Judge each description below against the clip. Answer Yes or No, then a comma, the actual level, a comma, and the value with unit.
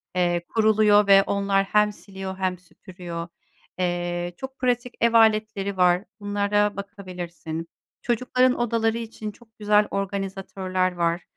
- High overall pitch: Yes, high, 200 Hz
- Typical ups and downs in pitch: Yes, average, 3.0 semitones